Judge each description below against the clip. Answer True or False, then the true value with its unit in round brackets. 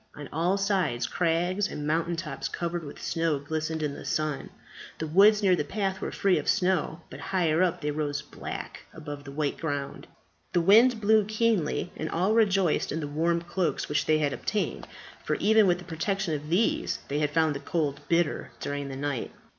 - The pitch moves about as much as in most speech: True (4.2 semitones)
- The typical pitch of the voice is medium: True (165 Hz)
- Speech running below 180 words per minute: False (195 wpm)